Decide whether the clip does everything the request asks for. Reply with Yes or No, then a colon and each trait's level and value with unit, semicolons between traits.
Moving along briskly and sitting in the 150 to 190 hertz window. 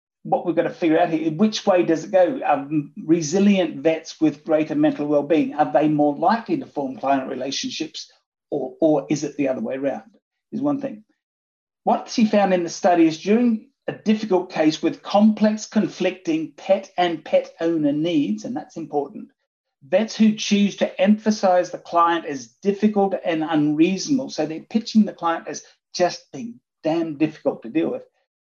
No: average, 175 wpm; medium, 185 Hz